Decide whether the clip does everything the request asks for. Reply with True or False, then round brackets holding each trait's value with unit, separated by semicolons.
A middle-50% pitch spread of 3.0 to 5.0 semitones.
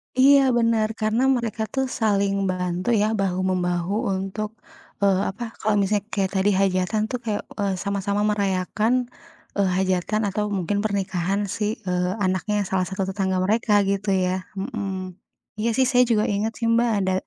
False (2.6 semitones)